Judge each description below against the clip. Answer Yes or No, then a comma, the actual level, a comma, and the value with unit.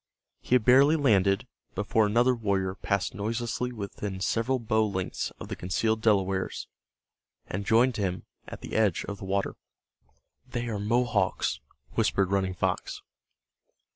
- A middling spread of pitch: Yes, average, 3.4 semitones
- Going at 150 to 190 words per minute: No, average, 140 wpm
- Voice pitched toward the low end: Yes, low, 105 Hz